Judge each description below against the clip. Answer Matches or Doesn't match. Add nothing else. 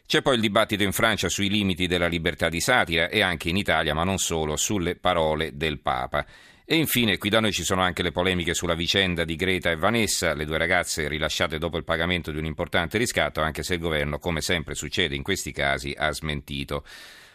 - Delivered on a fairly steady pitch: Doesn't match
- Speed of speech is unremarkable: Doesn't match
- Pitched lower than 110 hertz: Matches